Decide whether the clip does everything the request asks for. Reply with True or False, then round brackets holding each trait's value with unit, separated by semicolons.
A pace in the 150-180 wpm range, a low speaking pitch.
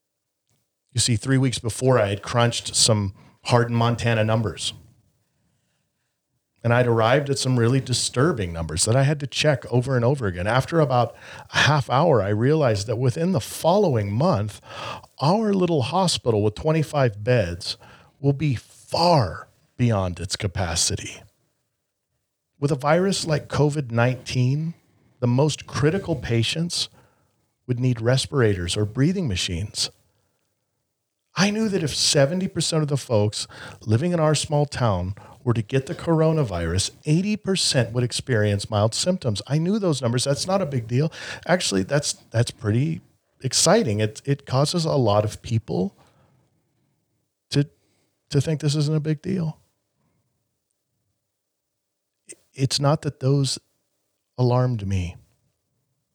False (135 wpm; 125 Hz)